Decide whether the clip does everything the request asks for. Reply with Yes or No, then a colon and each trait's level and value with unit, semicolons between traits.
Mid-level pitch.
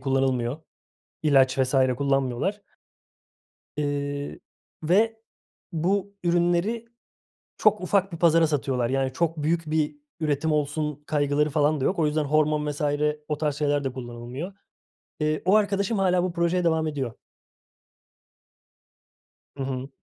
Yes: medium, 150 Hz